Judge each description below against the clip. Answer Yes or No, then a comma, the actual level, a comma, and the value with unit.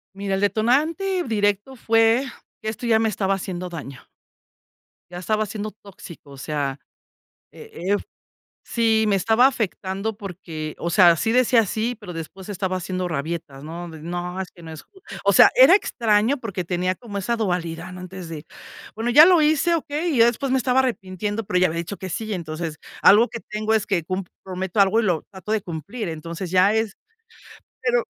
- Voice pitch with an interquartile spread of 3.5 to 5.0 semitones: Yes, average, 4.4 semitones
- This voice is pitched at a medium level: No, high, 200 Hz